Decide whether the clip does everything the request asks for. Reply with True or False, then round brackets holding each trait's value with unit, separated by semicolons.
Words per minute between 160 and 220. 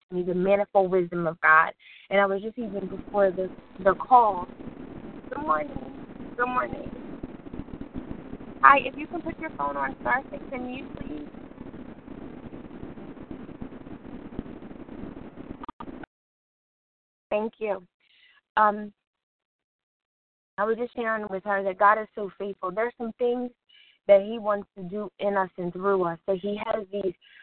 False (135 wpm)